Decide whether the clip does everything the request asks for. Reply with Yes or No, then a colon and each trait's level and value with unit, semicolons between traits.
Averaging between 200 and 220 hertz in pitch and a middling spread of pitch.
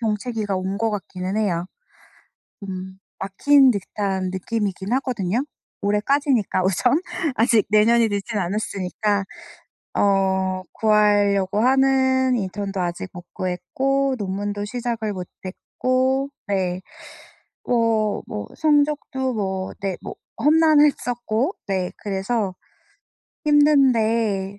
Yes: high, 210 Hz; average, 4.7 semitones